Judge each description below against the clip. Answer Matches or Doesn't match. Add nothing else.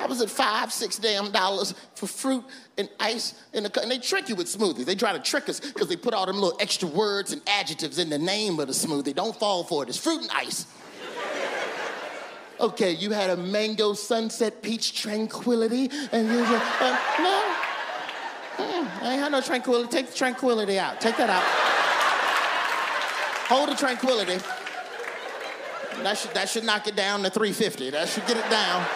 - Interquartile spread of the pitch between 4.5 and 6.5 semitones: Doesn't match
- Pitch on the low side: Doesn't match